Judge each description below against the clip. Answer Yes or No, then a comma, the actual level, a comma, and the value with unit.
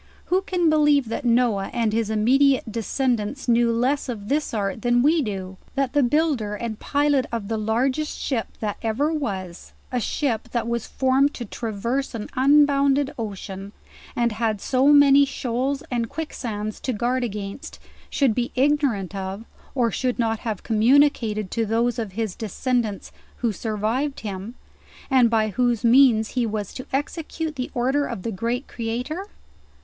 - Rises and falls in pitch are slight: No, average, 4.0 semitones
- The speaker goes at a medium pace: Yes, average, 165 wpm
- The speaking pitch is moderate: No, high, 240 Hz